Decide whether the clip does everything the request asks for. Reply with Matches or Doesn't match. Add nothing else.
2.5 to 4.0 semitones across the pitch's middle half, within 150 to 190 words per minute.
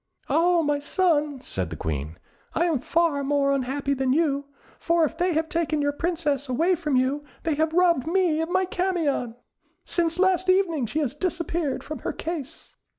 Matches